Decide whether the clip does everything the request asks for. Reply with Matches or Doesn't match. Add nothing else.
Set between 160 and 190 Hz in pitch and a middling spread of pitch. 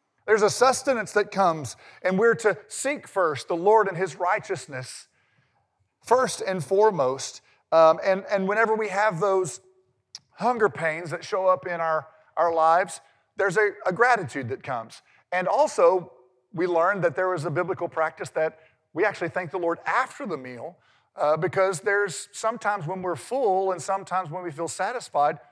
Matches